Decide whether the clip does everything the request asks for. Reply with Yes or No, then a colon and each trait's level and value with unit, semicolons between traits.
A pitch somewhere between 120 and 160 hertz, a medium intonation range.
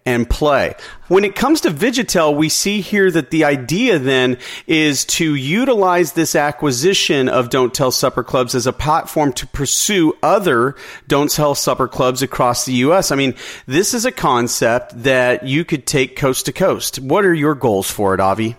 Yes: medium, 140 Hz; average, 4.6 semitones